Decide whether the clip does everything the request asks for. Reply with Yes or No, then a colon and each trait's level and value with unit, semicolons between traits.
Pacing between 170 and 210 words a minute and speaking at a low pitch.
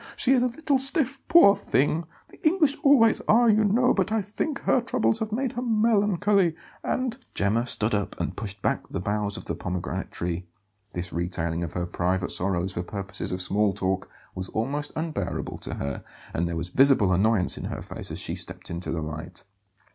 Yes: average, 200 wpm; low, 115 Hz